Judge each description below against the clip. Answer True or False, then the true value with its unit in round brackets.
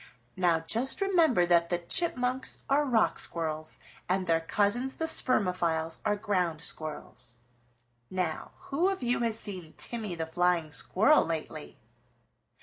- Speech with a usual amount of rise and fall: False (7.0 semitones)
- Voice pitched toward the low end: False (185 Hz)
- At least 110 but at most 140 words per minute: True (135 wpm)